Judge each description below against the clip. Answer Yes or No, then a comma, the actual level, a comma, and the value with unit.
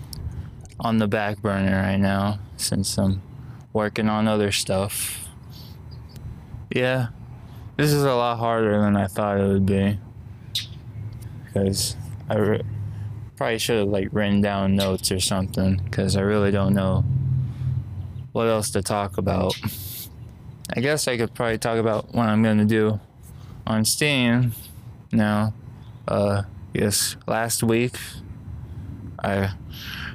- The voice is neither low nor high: No, low, 110 Hz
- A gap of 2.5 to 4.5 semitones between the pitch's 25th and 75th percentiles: Yes, average, 2.9 semitones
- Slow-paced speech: Yes, slow, 130 wpm